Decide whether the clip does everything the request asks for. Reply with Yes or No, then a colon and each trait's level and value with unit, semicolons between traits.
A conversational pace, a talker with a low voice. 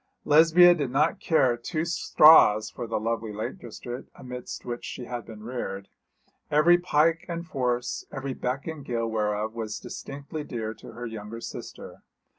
Yes: average, 160 wpm; low, 125 Hz